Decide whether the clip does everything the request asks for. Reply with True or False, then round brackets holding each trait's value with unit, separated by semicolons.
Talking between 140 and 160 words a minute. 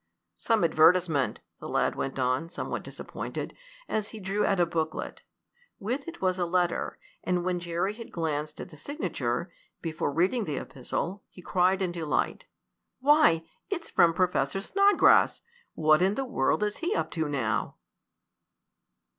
True (155 wpm)